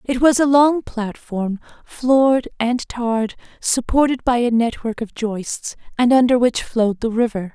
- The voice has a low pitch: No, high, 240 Hz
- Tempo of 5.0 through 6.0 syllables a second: No, 4.4 syllables/s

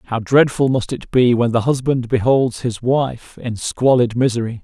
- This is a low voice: Yes, low, 125 Hz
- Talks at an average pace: Yes, average, 180 wpm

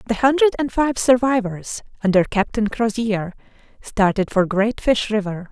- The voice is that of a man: No, female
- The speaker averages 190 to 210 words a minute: No, average, 140 wpm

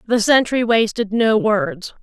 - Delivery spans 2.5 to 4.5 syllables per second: Yes, 3.9 syllables/s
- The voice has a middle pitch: No, high, 225 Hz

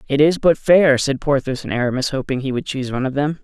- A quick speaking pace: Yes, fast, 260 wpm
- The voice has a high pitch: No, medium, 140 Hz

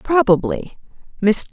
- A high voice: Yes, high, 240 Hz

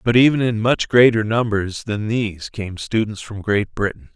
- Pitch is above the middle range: No, low, 110 Hz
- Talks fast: No, average, 190 wpm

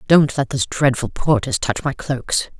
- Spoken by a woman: Yes, female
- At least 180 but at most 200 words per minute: Yes, average, 185 wpm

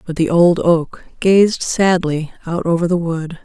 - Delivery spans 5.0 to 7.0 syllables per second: No, 3.9 syllables/s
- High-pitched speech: No, medium, 170 Hz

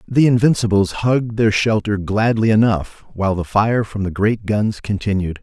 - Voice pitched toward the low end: Yes, low, 105 Hz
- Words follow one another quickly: No, average, 165 wpm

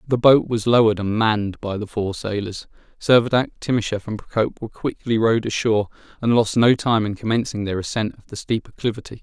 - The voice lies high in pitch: No, low, 110 Hz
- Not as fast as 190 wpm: No, average, 195 wpm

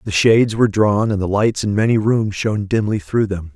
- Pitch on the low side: Yes, low, 105 Hz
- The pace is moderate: No, fast, 235 wpm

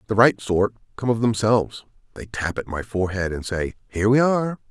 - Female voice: No, male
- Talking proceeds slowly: No, fast, 205 wpm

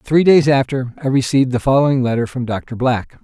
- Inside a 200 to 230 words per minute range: Yes, fast, 205 wpm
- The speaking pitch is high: No, low, 130 Hz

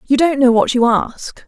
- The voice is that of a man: No, female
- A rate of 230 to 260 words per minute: Yes, fast, 245 wpm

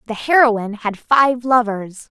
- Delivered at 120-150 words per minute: Yes, slow, 135 wpm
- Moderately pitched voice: No, high, 230 Hz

